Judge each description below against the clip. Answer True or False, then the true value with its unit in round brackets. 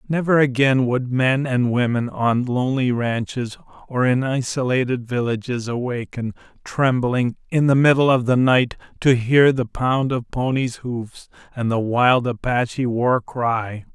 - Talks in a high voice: False (125 Hz)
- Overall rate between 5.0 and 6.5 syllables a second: False (4.2 syllables/s)